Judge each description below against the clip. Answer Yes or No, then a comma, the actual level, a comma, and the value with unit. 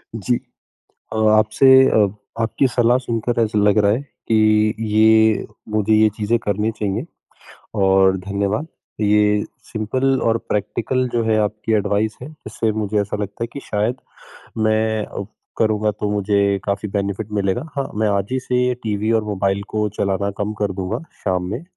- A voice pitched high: No, low, 105 Hz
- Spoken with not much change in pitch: Yes, narrow, 1.7 semitones